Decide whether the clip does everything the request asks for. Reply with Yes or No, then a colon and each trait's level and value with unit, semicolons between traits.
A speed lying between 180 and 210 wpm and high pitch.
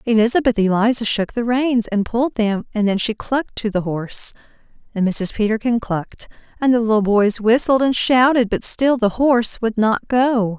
Yes: average, 185 wpm; high, 225 Hz